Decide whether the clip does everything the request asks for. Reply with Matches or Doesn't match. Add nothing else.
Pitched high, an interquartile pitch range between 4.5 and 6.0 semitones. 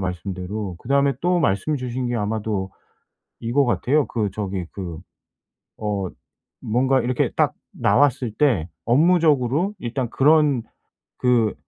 Doesn't match